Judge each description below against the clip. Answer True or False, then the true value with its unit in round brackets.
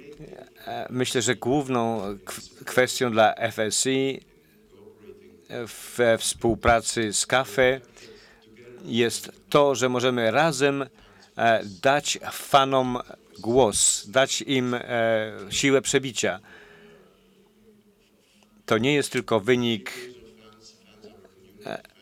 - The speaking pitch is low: True (125 Hz)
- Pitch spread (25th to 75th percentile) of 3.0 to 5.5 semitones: True (3.3 semitones)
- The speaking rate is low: True (75 wpm)